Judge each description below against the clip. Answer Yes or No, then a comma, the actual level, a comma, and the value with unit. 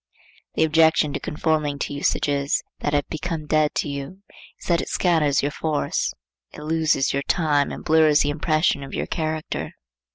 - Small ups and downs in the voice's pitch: Yes, narrow, 1.7 semitones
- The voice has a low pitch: No, medium, 150 Hz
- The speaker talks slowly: No, average, 170 wpm